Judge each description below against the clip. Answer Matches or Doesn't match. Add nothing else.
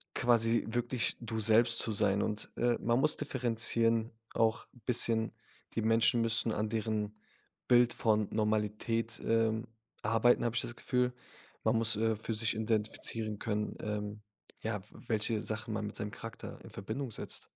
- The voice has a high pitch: Doesn't match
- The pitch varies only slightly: Matches